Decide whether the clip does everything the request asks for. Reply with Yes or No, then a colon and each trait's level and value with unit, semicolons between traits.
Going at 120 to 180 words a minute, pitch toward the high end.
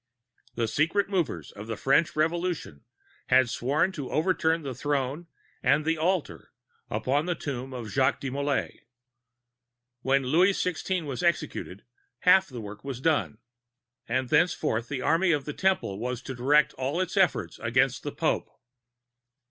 No: average, 150 wpm; medium, 145 Hz